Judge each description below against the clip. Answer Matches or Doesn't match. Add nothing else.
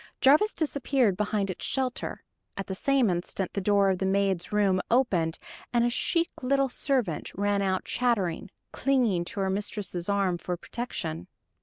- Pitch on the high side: Matches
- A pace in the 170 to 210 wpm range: Doesn't match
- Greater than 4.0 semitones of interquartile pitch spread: Matches